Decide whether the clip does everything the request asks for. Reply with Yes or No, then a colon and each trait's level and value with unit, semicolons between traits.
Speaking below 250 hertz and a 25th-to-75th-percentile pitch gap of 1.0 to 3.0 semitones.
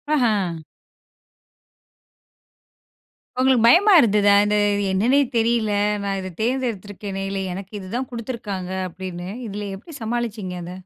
No: high, 210 Hz; average, 3.8 semitones